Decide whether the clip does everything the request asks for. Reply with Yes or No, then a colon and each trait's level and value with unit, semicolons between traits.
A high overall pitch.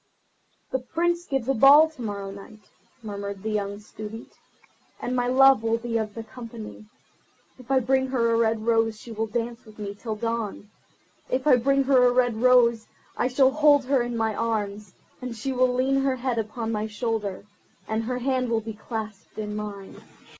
Yes: high, 230 Hz